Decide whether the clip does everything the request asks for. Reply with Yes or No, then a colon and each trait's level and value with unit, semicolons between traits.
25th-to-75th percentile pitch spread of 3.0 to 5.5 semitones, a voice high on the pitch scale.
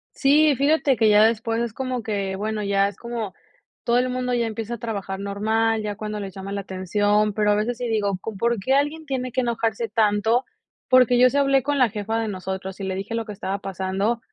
Yes: average, 3.4 semitones; high, 220 Hz